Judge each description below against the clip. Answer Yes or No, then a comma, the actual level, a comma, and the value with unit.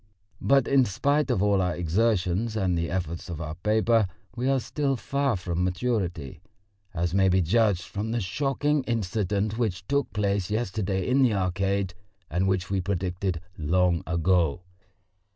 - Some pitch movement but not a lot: Yes, average, 4.3 semitones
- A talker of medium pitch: No, very low, 95 Hz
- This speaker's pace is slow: No, average, 155 wpm